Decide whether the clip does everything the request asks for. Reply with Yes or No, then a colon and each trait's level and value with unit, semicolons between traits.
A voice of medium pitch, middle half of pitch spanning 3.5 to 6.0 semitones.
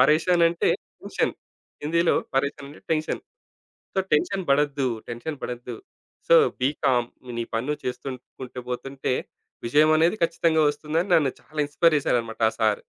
Yes: medium, 145 Hz; average, 4.2 semitones